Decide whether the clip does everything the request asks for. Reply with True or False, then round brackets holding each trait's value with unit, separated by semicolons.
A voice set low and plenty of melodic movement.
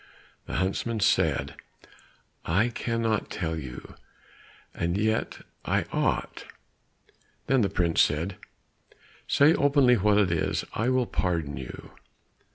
True (100 Hz; 5.7 semitones)